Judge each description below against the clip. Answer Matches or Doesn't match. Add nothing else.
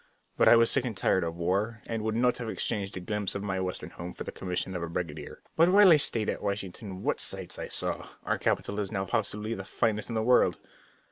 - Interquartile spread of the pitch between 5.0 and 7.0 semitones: Doesn't match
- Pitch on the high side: Doesn't match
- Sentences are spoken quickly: Matches